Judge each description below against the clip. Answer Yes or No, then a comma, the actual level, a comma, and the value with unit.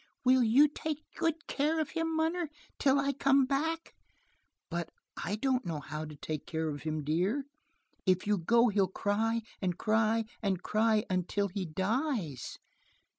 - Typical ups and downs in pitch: No, wide, 7.5 semitones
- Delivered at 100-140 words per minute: No, average, 160 wpm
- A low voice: No, high, 220 Hz